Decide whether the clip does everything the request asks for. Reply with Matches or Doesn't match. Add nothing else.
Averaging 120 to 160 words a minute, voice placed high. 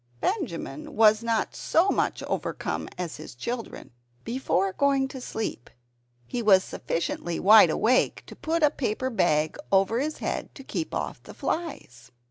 Matches